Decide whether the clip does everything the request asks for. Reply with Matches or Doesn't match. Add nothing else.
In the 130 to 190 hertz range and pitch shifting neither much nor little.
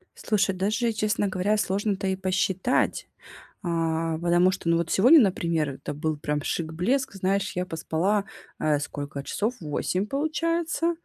Matches